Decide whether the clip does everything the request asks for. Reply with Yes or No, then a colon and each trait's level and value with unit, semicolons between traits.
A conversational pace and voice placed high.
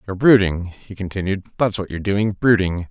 No: average, 185 wpm; low, 100 Hz